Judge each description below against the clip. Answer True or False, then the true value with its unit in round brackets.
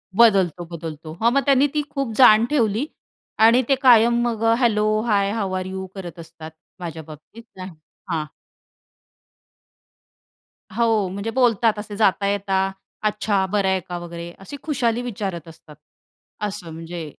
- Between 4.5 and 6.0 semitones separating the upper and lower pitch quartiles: True (4.8 semitones)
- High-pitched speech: True (200 Hz)